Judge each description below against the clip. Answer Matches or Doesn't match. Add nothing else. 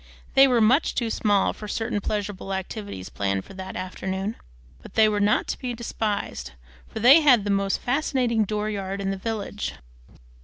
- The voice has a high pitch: Matches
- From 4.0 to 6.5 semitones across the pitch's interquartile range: Doesn't match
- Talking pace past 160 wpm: Matches